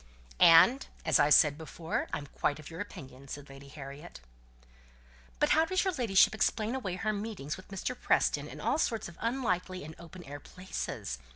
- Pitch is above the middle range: No, medium, 180 Hz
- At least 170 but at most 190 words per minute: Yes, average, 180 wpm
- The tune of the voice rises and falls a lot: Yes, wide, 7.0 semitones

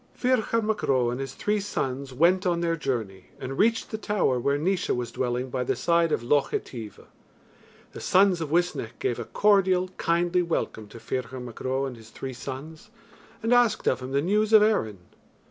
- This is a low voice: No, medium, 145 Hz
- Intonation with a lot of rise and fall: Yes, wide, 6.9 semitones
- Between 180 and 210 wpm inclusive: Yes, average, 195 wpm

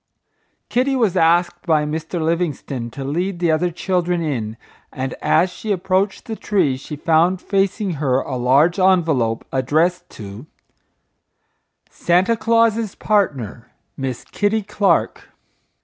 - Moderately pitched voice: Yes, medium, 170 Hz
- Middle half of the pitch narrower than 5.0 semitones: No, wide, 5.5 semitones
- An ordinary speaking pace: No, slow, 125 wpm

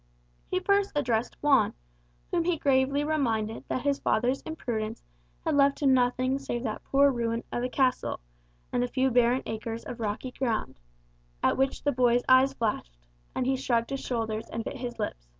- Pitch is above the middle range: Yes, very high, 255 Hz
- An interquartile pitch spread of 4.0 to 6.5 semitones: No, average, 3.0 semitones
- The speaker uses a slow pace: No, average, 180 wpm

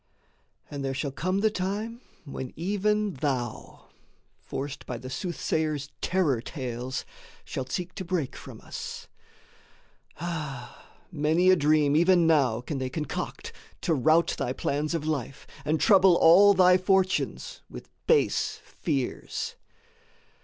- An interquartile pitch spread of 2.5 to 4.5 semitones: No, average, 5.2 semitones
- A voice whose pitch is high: No, medium, 155 Hz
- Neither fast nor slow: No, slow, 130 wpm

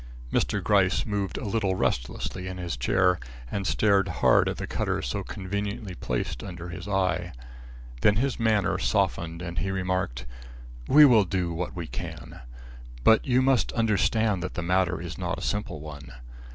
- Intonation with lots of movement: No, average, 2.8 semitones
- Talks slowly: No, average, 165 wpm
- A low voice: Yes, very low, 95 Hz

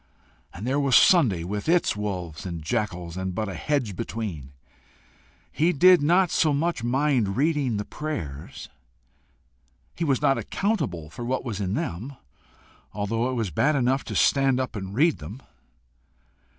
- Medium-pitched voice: No, low, 120 Hz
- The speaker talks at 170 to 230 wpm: No, average, 155 wpm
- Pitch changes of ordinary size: No, wide, 7.1 semitones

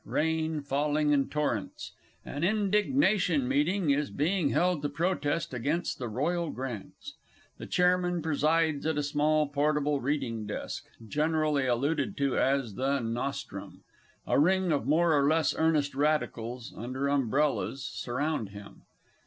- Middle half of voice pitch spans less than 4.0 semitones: Yes, average, 3.0 semitones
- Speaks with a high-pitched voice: No, medium, 145 Hz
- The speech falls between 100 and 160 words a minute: Yes, slow, 135 wpm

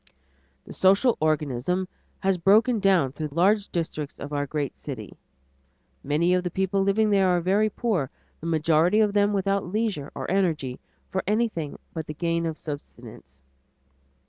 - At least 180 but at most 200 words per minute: No, average, 155 wpm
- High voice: No, medium, 180 Hz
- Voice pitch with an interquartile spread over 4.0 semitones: Yes, average, 4.5 semitones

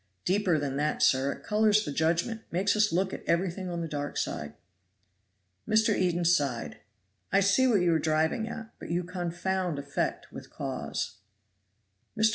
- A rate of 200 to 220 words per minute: No, average, 165 wpm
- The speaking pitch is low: No, medium, 175 Hz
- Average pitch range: Yes, average, 4.2 semitones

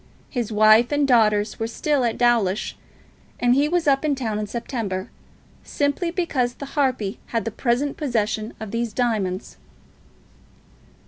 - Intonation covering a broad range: No, average, 4.4 semitones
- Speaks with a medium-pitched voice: No, high, 235 Hz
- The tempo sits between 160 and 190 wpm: No, average, 145 wpm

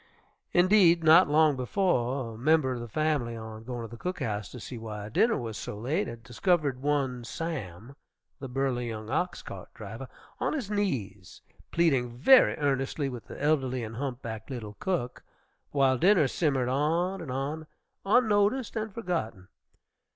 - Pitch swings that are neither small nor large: No, wide, 5.9 semitones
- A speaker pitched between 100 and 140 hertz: Yes, low, 135 Hz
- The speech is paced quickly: No, average, 160 wpm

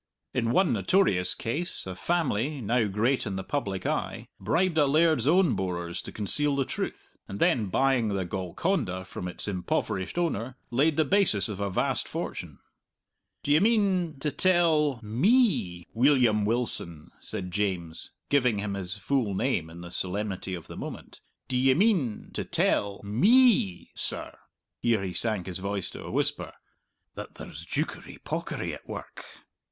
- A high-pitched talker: No, low, 115 Hz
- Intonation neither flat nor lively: No, wide, 7.8 semitones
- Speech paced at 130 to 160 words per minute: Yes, average, 155 wpm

